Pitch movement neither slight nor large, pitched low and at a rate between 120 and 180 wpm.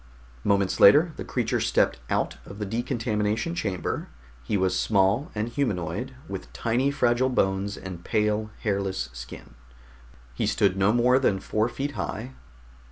Yes: average, 4.0 semitones; low, 105 Hz; average, 145 wpm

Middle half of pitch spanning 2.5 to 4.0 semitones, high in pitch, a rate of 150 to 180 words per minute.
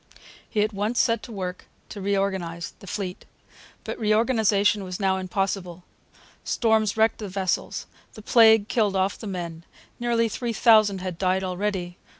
Yes: average, 2.9 semitones; high, 200 Hz; average, 155 wpm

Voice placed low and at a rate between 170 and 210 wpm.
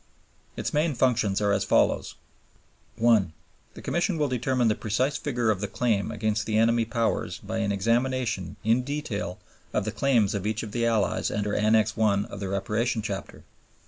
Yes: low, 110 Hz; average, 175 wpm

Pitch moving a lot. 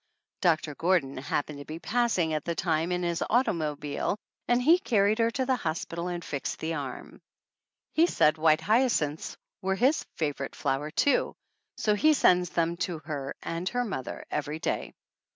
Yes: wide, 5.9 semitones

